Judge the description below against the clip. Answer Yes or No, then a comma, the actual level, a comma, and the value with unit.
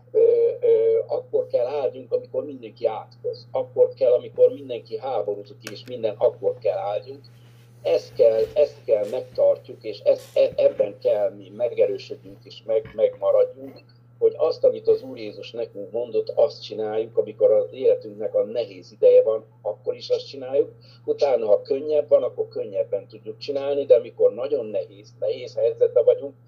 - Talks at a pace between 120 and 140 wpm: No, fast, 155 wpm